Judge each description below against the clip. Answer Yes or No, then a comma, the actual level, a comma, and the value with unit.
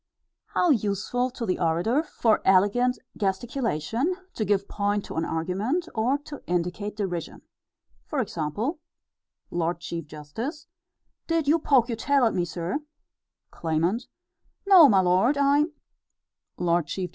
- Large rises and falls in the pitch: Yes, wide, 7.1 semitones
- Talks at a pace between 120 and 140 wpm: Yes, slow, 135 wpm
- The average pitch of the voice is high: Yes, high, 210 Hz